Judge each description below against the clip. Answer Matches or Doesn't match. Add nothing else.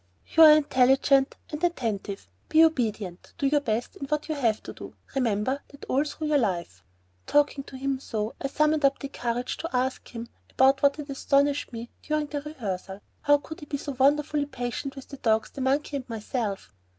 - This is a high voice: Matches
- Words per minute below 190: Doesn't match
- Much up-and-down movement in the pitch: Doesn't match